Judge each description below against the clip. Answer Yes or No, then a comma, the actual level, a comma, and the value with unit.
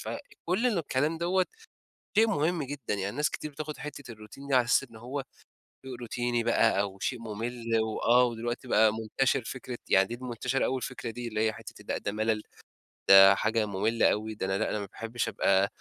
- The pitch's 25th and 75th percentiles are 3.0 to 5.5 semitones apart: Yes, average, 3.7 semitones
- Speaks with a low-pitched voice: Yes, low, 120 Hz